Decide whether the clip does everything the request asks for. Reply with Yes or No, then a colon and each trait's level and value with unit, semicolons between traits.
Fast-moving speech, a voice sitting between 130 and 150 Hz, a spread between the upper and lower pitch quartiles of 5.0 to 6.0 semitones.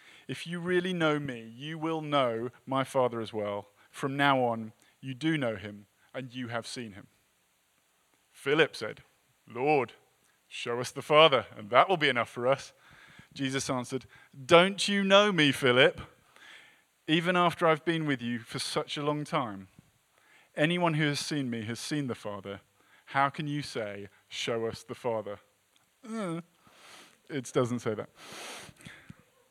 No: average, 155 wpm; low, 135 Hz; average, 5.3 semitones